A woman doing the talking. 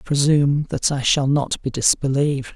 No: male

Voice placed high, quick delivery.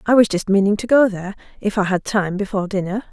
Yes: high, 200 Hz; fast, 250 wpm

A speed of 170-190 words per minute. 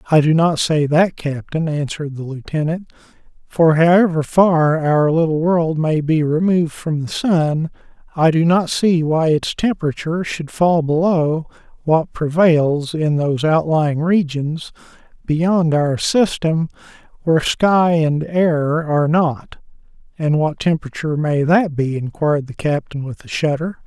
No: average, 145 wpm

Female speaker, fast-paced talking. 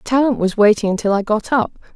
Yes: female; fast, 215 wpm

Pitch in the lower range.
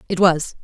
No: medium, 175 Hz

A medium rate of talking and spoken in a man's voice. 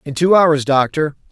Yes: average, 185 wpm; male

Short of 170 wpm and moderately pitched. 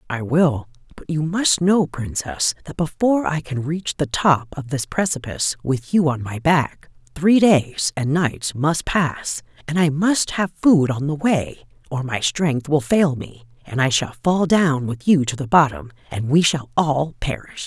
No: average, 195 wpm; medium, 145 Hz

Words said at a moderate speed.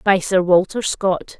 Yes: average, 170 wpm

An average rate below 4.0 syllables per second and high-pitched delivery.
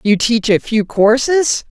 Yes: 3.8 syllables/s; high, 235 Hz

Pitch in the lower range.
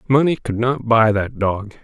Yes: low, 115 Hz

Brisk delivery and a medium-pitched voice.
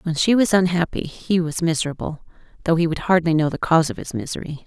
Yes: fast, 220 wpm; medium, 170 Hz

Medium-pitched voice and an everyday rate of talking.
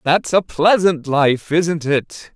Yes: medium, 160 Hz; average, 155 wpm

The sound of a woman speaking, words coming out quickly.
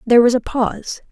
Yes: female; fast, 215 wpm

